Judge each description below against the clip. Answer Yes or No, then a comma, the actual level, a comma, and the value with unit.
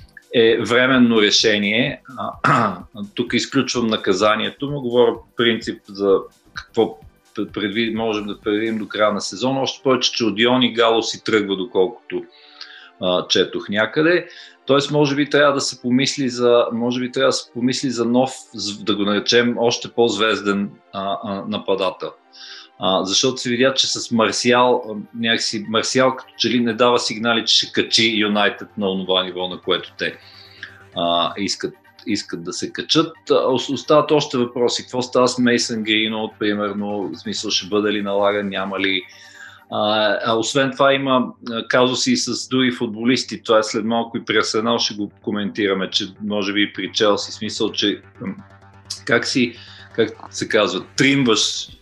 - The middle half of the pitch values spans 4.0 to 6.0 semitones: No, average, 3.4 semitones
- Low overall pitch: Yes, low, 115 Hz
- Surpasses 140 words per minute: Yes, average, 155 wpm